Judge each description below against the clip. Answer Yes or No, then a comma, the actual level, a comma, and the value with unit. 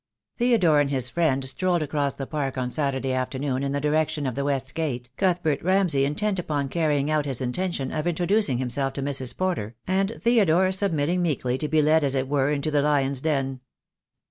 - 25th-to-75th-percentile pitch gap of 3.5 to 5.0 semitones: Yes, average, 4.1 semitones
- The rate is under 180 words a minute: No, average, 195 wpm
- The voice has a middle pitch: Yes, medium, 145 Hz